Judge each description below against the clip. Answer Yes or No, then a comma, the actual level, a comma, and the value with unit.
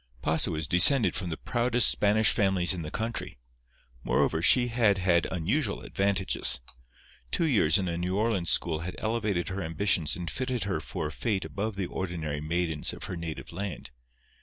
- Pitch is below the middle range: Yes, very low, 95 Hz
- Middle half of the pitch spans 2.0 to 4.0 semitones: No, average, 4.4 semitones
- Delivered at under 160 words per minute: No, average, 175 wpm